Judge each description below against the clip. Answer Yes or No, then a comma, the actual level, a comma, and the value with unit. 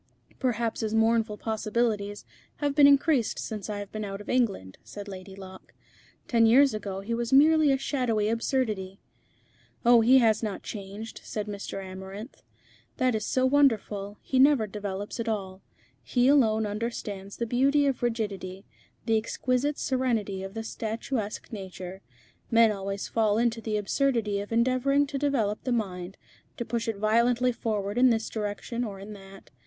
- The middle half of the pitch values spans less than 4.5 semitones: Yes, average, 3.4 semitones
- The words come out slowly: No, average, 165 wpm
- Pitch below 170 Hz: No, high, 220 Hz